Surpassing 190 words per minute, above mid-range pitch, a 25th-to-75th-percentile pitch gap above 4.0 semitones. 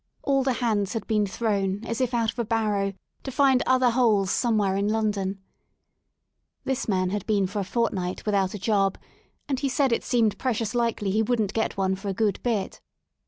No: average, 200 wpm; high, 215 Hz; average, 3.3 semitones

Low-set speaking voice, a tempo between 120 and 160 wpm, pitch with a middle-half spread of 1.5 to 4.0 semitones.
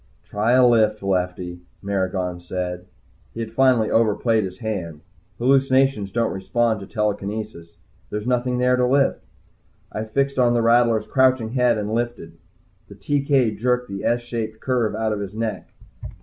Yes: low, 110 Hz; average, 155 wpm; average, 3.7 semitones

